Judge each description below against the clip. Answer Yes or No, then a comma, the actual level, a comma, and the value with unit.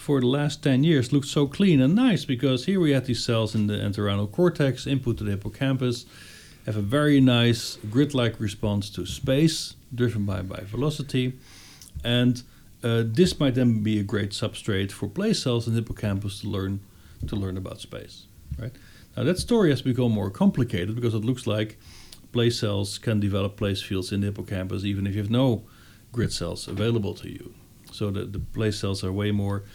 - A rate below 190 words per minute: No, average, 195 wpm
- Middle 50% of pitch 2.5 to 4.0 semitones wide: No, average, 4.4 semitones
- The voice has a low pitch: Yes, low, 110 Hz